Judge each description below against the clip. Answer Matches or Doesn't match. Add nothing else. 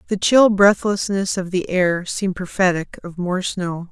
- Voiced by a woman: Matches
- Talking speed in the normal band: Matches